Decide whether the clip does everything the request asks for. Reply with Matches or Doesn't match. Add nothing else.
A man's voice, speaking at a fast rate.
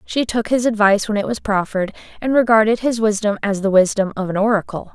Doesn't match